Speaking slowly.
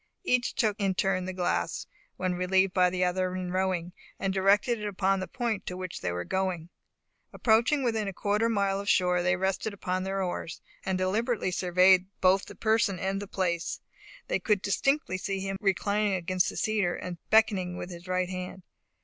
No: average, 195 wpm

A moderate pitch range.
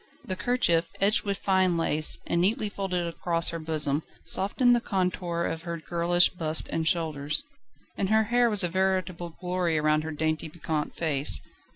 Yes: average, 3.1 semitones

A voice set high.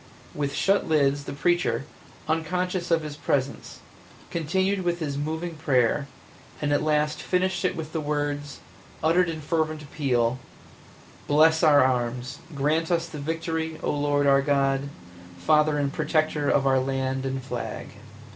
No: medium, 150 Hz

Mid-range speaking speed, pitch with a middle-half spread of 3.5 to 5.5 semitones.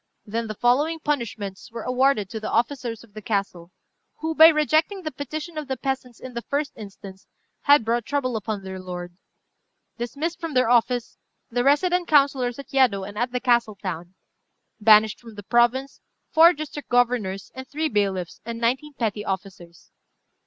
Yes: average, 170 wpm; average, 5.2 semitones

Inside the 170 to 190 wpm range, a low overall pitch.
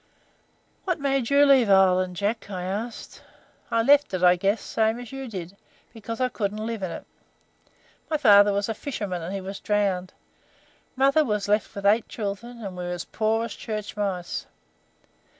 No: average, 180 wpm; high, 210 Hz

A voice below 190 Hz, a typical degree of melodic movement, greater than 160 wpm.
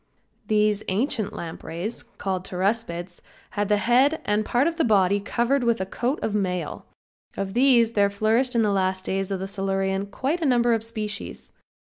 No: high, 210 Hz; average, 3.6 semitones; average, 175 wpm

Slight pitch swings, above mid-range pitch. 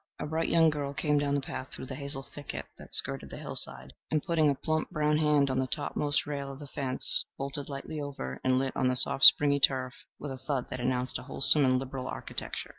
No: narrow, 2.1 semitones; medium, 140 Hz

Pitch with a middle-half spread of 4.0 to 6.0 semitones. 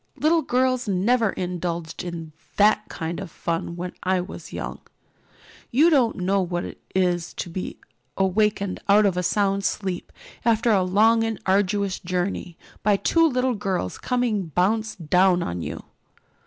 No: average, 3.6 semitones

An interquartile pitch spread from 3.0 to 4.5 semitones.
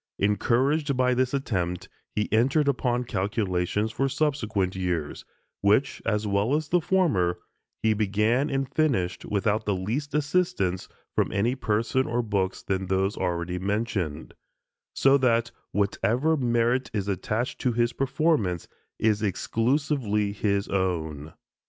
No: average, 5.3 semitones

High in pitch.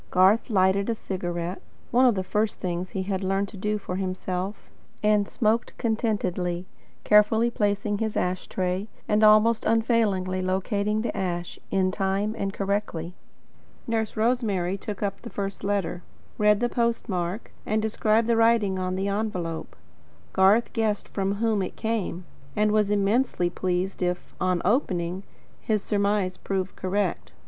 Yes: high, 200 Hz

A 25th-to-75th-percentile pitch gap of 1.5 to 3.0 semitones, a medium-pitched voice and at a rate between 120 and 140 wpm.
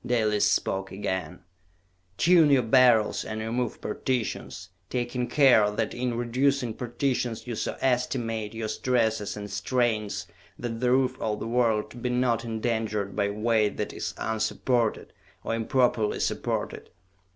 No: narrow, 2.5 semitones; low, 115 Hz; slow, 135 wpm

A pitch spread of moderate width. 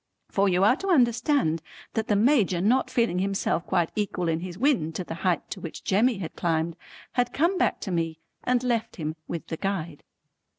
No: wide, 6.4 semitones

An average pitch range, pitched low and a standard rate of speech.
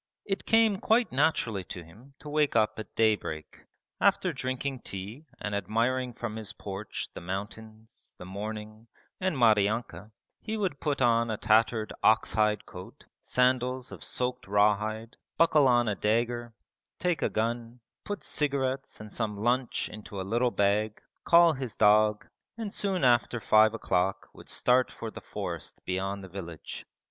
Yes: average, 3.6 semitones; low, 115 Hz; average, 155 wpm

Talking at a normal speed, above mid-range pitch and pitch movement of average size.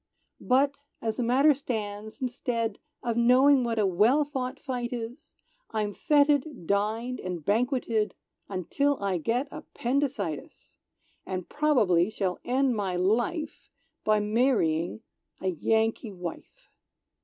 No: slow, 120 wpm; high, 230 Hz; average, 4.4 semitones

